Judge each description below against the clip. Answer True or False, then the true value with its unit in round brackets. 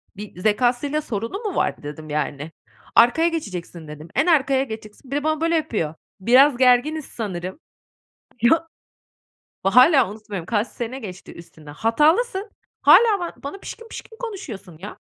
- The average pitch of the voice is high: True (245 Hz)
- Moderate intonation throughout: False (8.6 semitones)